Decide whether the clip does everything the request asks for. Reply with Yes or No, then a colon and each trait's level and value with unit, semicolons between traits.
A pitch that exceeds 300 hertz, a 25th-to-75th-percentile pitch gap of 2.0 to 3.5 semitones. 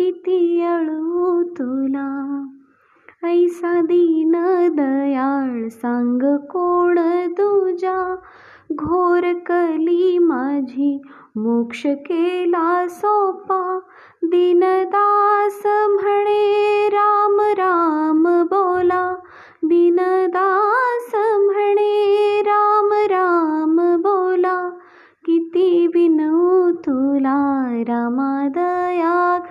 Yes: very high, 350 Hz; average, 3.1 semitones